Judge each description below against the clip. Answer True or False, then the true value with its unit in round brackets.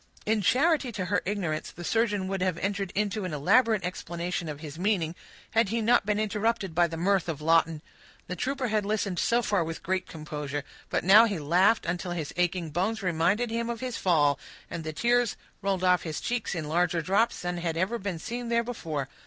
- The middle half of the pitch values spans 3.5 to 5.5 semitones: True (4.7 semitones)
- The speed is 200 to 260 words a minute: True (205 wpm)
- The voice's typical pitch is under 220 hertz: True (185 Hz)